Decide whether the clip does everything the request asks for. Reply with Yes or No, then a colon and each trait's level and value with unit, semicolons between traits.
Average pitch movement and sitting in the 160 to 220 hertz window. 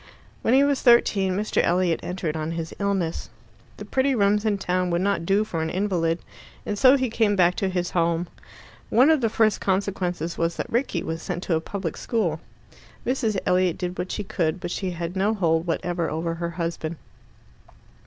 Yes: average, 3.6 semitones; medium, 185 Hz